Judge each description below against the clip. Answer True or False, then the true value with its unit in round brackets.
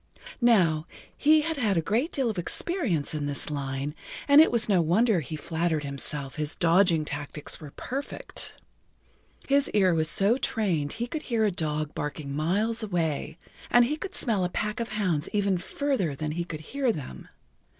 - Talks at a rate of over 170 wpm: True (180 wpm)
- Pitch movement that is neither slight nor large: False (7.2 semitones)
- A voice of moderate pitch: True (180 Hz)